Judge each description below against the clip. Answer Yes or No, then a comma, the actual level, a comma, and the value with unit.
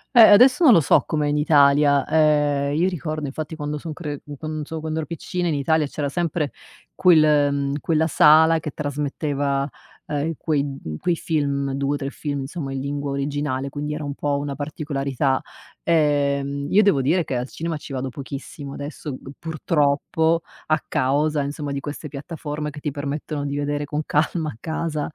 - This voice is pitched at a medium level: Yes, medium, 145 Hz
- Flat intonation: Yes, narrow, 1.9 semitones